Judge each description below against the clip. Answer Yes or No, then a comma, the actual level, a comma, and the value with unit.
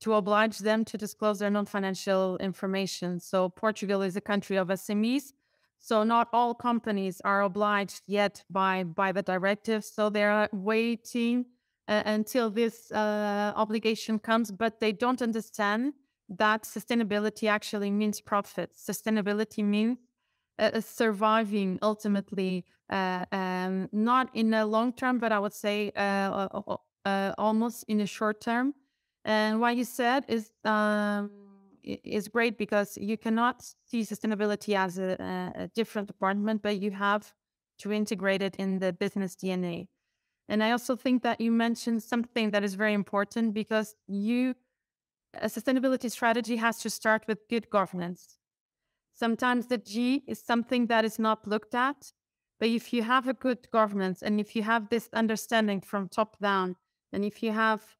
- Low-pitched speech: No, high, 215 Hz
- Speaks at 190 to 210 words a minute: No, average, 155 wpm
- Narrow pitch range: Yes, narrow, 2.3 semitones